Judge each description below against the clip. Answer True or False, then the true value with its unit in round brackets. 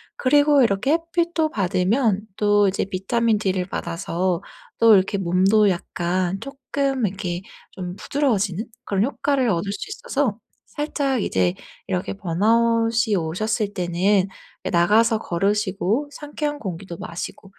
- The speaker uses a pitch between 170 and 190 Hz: False (205 Hz)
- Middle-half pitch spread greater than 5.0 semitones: True (5.6 semitones)